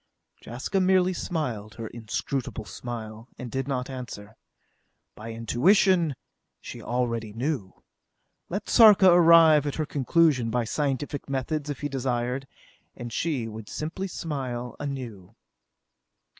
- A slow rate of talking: Yes, slow, 120 wpm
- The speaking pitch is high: No, low, 130 Hz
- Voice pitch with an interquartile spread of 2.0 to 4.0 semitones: No, average, 5.1 semitones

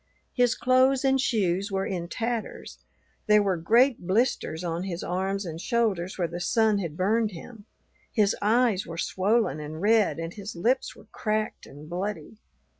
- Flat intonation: No, average, 4.6 semitones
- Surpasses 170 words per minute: No, average, 165 wpm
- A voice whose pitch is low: No, high, 200 Hz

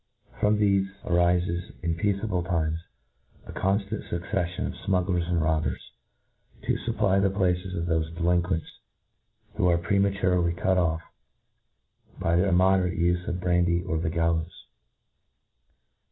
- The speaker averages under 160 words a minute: Yes, slow, 135 wpm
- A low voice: Yes, very low, 90 Hz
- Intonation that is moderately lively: No, narrow, 2.1 semitones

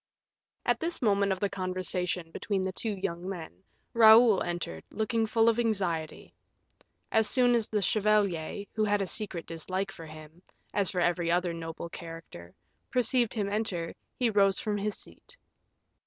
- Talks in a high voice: Yes, high, 195 Hz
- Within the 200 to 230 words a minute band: No, average, 160 wpm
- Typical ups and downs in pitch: Yes, average, 4.1 semitones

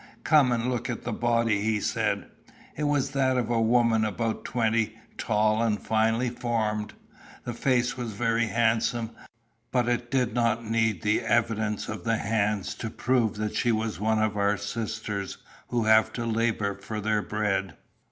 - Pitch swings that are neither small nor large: No, narrow, 1.9 semitones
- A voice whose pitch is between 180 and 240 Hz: No, low, 115 Hz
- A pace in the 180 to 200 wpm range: No, average, 170 wpm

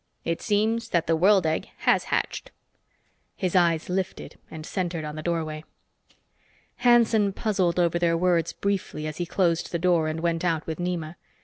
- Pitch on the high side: No, medium, 175 Hz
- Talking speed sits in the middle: Yes, average, 170 wpm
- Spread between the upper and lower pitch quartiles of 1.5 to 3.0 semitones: Yes, average, 2.7 semitones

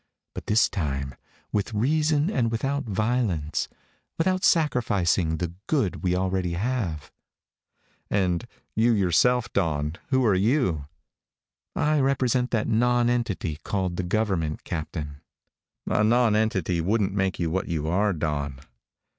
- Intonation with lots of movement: Yes, wide, 6.1 semitones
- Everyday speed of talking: No, slow, 120 wpm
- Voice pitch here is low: Yes, low, 100 Hz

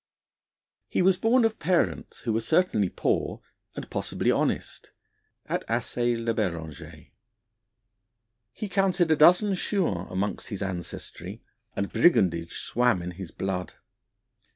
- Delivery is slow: Yes, slow, 125 wpm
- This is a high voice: No, low, 115 Hz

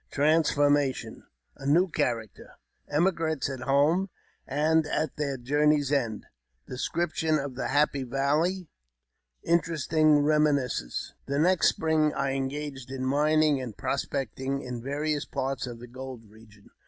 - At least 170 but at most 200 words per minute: No, average, 140 wpm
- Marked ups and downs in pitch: No, average, 2.9 semitones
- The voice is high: No, medium, 140 Hz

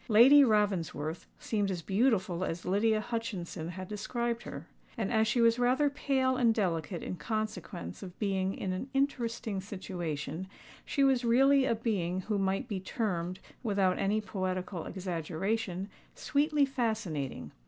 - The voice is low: No, high, 205 Hz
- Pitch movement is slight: No, average, 4.2 semitones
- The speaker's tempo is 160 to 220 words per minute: No, average, 145 wpm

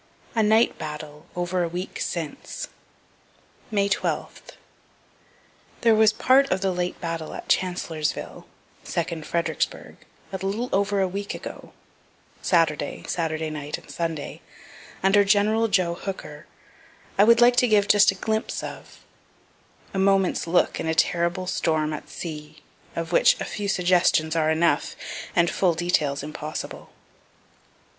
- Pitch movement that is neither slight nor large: Yes, average, 3.9 semitones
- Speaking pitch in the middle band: Yes, medium, 180 Hz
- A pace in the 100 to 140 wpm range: Yes, slow, 135 wpm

